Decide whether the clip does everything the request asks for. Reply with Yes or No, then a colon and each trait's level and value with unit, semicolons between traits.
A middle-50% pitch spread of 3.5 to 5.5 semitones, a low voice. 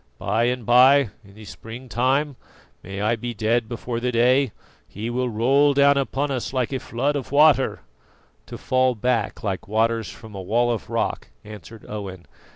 No: average, 3.1 semitones; low, 120 Hz